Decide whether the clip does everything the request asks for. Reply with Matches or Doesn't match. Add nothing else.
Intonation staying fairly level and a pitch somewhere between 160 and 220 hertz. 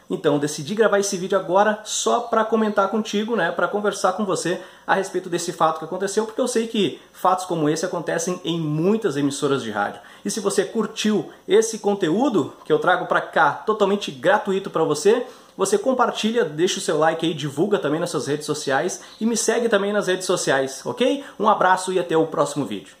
Doesn't match